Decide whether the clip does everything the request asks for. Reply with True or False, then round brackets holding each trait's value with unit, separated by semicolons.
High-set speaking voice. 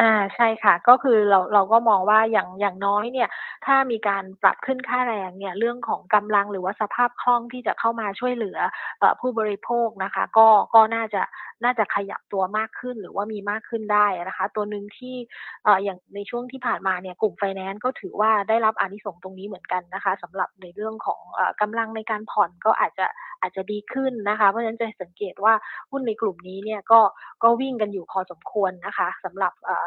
True (210 Hz)